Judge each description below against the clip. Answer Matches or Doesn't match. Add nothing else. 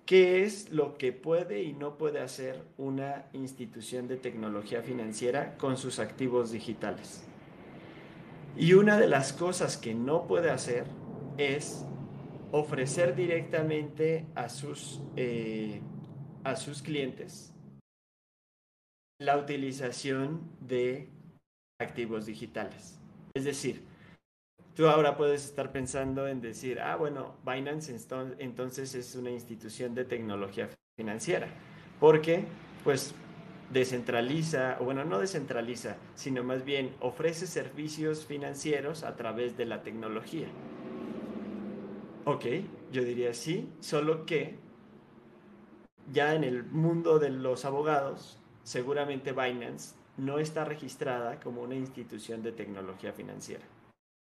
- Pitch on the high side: Doesn't match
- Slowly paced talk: Matches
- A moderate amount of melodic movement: Matches